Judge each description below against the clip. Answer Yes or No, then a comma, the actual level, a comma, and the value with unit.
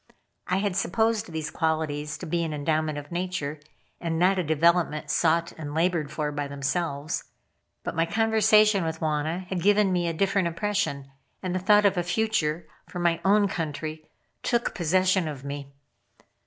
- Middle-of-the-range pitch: Yes, medium, 170 Hz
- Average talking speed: Yes, average, 170 wpm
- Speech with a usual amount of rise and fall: Yes, average, 3.6 semitones